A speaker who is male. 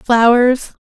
No: female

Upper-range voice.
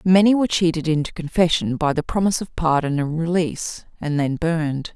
No: medium, 165 Hz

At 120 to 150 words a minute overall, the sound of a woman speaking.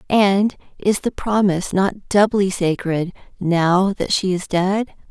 Yes: average, 140 wpm; female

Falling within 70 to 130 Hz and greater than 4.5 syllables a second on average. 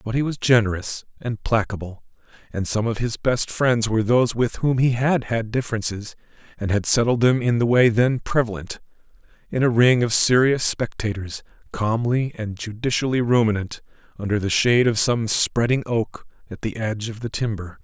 Yes: low, 115 Hz; 5.2 syllables/s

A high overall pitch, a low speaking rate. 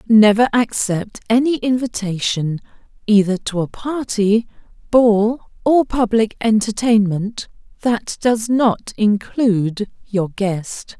Yes: high, 215 Hz; slow, 100 wpm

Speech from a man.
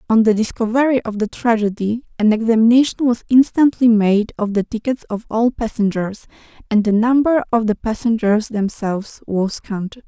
No: female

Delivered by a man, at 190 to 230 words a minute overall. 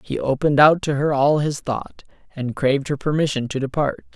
Yes: male; average, 200 wpm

